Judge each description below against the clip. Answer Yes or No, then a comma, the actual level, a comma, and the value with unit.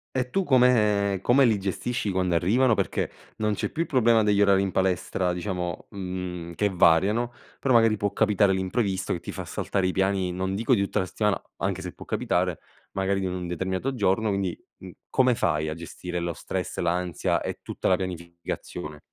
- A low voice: Yes, very low, 95 Hz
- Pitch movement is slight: No, average, 3.2 semitones